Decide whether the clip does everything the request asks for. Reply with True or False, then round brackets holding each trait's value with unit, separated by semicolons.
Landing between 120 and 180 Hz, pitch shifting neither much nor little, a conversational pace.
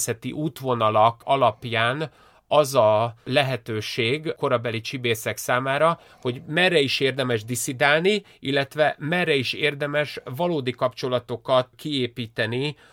False (130 Hz; 3.6 semitones; 95 wpm)